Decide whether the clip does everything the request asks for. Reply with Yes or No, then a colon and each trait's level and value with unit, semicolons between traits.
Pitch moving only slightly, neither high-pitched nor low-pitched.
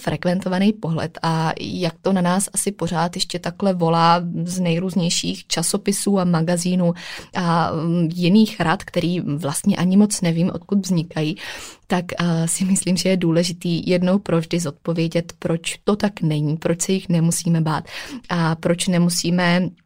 Yes: narrow, 1.9 semitones; medium, 175 Hz